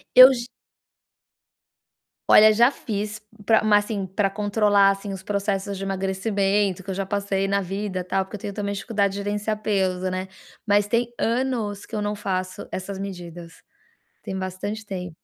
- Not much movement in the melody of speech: Yes, narrow, 1.6 semitones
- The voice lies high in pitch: Yes, high, 200 Hz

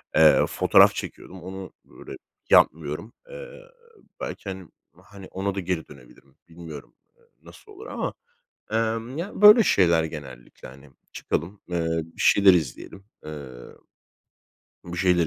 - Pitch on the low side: Yes, very low, 90 Hz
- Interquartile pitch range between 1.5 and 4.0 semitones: No, average, 4.5 semitones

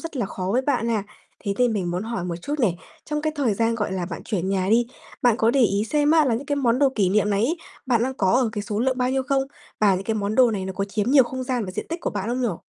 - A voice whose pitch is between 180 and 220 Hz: No, high, 230 Hz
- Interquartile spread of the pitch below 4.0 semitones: No, average, 4.6 semitones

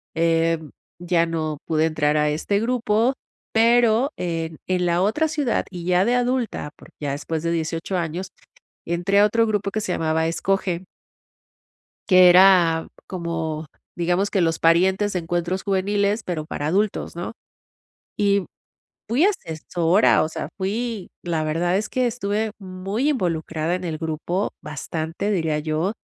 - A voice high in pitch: No, medium, 180 Hz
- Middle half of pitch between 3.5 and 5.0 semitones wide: Yes, average, 4.0 semitones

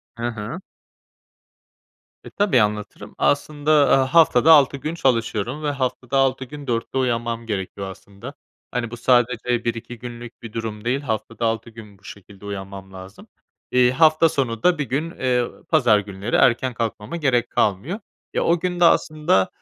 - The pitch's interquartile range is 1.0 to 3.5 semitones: No, average, 4.4 semitones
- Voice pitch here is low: Yes, low, 120 Hz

